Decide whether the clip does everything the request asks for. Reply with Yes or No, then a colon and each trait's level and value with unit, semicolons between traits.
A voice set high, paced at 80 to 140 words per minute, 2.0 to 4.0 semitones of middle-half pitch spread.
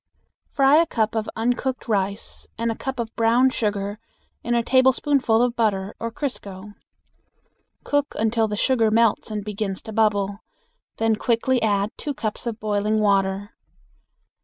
No: high, 220 Hz; average, 150 wpm; average, 2.7 semitones